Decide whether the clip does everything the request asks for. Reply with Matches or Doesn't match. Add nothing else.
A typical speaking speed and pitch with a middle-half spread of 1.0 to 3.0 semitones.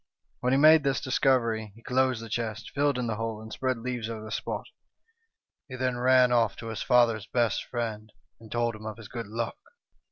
Doesn't match